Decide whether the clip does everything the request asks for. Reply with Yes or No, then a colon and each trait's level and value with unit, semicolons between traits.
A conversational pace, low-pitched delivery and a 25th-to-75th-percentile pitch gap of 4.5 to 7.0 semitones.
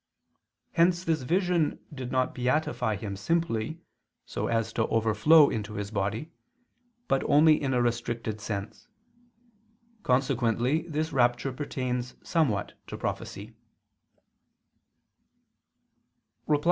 No: slow, 100 wpm; low, 125 Hz; wide, 5.5 semitones